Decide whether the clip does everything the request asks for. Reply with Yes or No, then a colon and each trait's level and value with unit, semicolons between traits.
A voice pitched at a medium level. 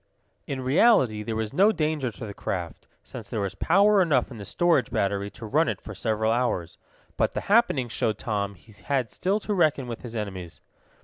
No: low, 120 Hz